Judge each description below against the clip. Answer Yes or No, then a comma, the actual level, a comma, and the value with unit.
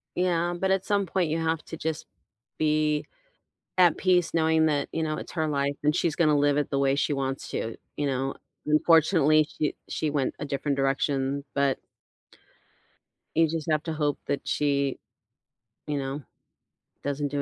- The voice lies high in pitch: No, medium, 150 Hz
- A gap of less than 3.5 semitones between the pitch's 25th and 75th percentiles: Yes, narrow, 2.4 semitones